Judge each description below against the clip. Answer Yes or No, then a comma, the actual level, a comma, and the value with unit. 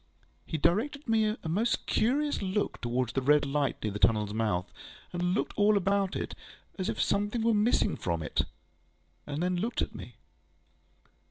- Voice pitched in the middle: Yes, medium, 180 Hz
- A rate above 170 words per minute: No, average, 165 wpm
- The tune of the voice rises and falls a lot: Yes, wide, 8.6 semitones